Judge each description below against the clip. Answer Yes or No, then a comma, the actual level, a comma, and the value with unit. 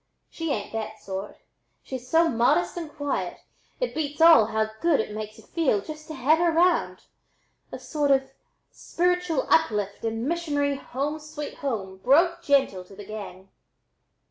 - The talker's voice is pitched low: No, very high, 280 Hz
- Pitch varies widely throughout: Yes, wide, 6.8 semitones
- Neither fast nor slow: Yes, average, 160 wpm